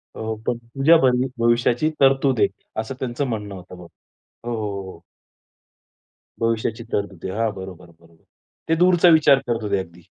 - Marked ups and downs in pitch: Yes, wide, 5.7 semitones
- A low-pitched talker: Yes, low, 115 Hz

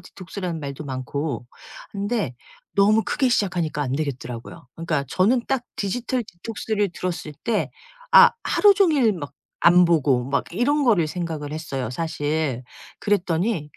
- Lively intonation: Yes, wide, 6.5 semitones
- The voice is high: No, medium, 175 Hz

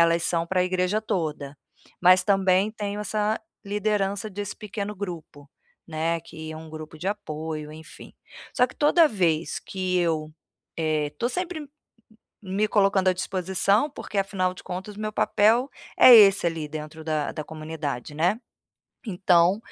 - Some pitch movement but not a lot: Yes, average, 4.5 semitones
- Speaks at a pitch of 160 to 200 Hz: Yes, medium, 185 Hz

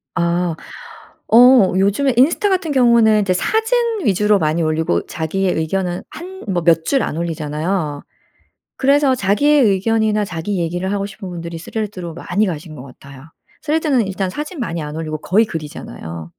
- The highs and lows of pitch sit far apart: Yes, wide, 5.7 semitones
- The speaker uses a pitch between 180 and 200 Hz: Yes, high, 190 Hz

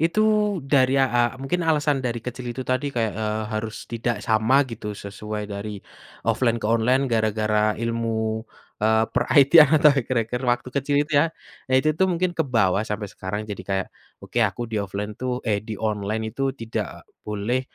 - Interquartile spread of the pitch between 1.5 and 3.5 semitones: No, average, 4.0 semitones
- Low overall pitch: Yes, low, 115 Hz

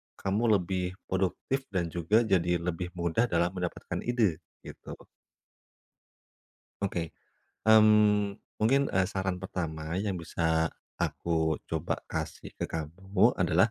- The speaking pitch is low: Yes, very low, 90 Hz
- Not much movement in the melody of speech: No, average, 3.5 semitones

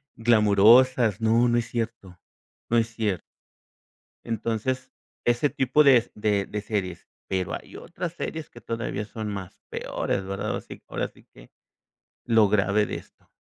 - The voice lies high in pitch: No, low, 110 Hz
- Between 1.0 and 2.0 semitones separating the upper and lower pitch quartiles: No, average, 2.8 semitones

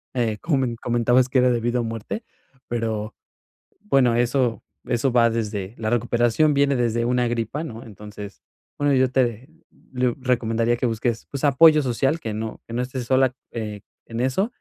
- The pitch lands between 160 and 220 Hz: No, low, 120 Hz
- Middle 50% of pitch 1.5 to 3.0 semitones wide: Yes, narrow, 2.4 semitones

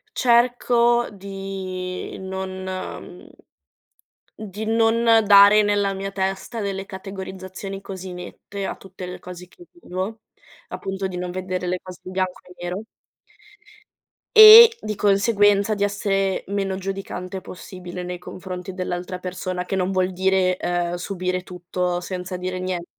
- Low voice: No, high, 190 Hz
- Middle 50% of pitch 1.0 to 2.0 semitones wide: Yes, narrow, 1.6 semitones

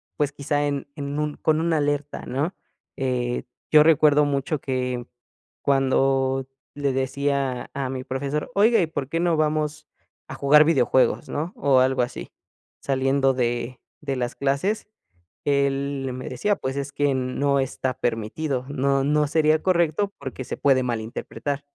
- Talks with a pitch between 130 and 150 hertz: Yes, medium, 140 Hz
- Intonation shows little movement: Yes, narrow, 2.3 semitones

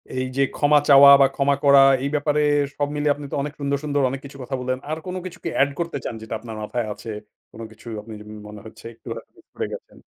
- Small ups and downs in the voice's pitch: No, average, 3.3 semitones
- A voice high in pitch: No, medium, 140 Hz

